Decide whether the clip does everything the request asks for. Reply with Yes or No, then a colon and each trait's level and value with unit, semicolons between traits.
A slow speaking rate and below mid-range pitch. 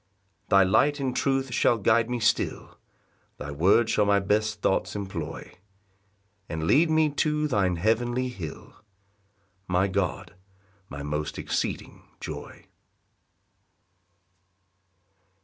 Yes: slow, 115 wpm; low, 105 Hz